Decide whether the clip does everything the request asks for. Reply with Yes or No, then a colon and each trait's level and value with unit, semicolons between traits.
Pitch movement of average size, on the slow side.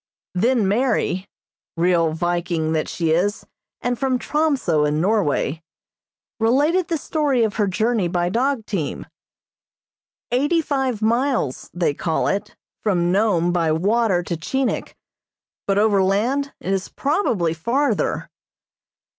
No: wide, 6.6 semitones; slow, 120 wpm